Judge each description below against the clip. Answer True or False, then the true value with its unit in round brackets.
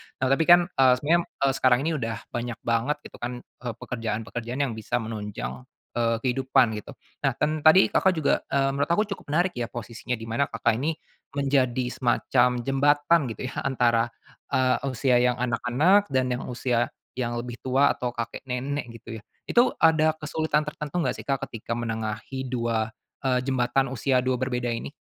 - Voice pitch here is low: True (125 Hz)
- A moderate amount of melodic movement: True (3.0 semitones)